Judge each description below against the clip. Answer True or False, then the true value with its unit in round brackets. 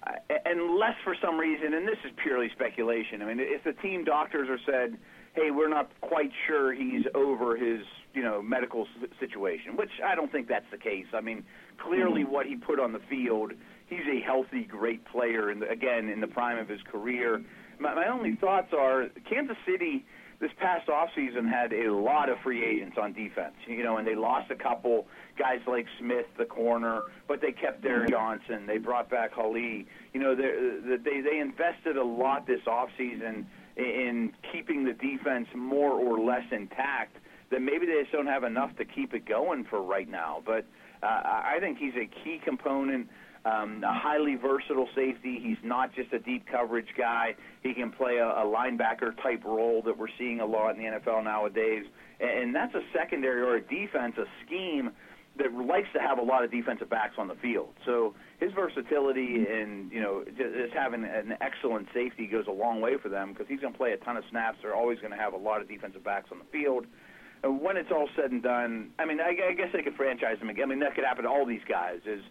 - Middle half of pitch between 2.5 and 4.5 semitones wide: False (5.0 semitones)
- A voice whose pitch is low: True (125 Hz)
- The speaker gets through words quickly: True (210 wpm)